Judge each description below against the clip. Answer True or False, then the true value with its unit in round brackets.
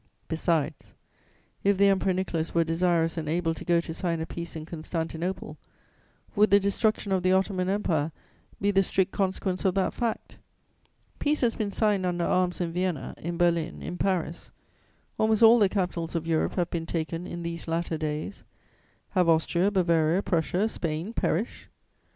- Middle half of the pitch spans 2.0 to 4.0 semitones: True (2.9 semitones)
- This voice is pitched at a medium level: True (175 Hz)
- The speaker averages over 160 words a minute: True (170 wpm)